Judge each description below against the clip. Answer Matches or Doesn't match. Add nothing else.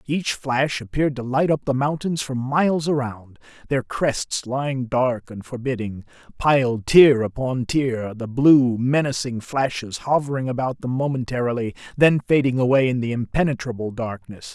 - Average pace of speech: Matches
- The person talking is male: Matches